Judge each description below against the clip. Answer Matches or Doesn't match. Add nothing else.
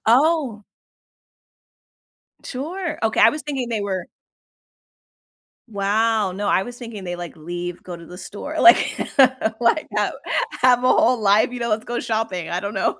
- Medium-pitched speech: Doesn't match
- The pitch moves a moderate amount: Matches